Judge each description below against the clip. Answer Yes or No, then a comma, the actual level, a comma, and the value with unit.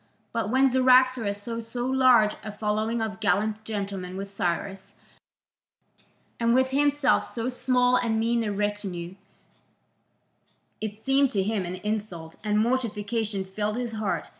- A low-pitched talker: No, high, 220 Hz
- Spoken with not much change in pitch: No, average, 3.4 semitones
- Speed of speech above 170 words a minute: No, average, 140 wpm